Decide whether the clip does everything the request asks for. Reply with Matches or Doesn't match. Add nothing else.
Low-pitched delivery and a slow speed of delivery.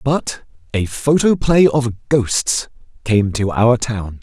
Matches